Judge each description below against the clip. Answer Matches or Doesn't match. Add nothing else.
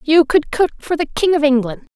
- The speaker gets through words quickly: Matches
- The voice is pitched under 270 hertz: Doesn't match